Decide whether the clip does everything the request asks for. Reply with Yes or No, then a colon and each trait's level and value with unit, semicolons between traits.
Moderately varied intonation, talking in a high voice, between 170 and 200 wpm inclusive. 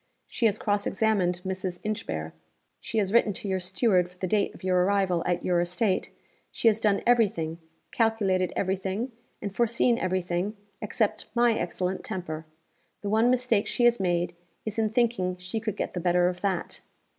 Yes: average, 3.4 semitones; high, 195 Hz; average, 185 wpm